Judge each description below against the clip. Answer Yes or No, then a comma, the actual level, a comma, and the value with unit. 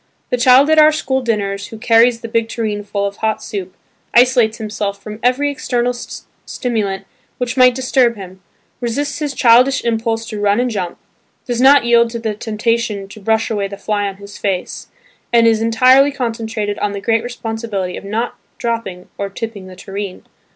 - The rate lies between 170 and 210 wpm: Yes, average, 180 wpm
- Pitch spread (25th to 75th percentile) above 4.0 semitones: No, average, 3.1 semitones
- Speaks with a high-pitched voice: Yes, high, 225 Hz